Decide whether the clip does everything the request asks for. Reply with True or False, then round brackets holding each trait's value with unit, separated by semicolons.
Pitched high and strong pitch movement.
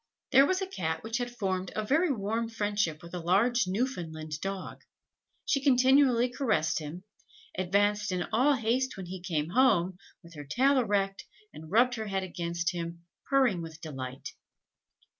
True (200 Hz; 6.2 semitones)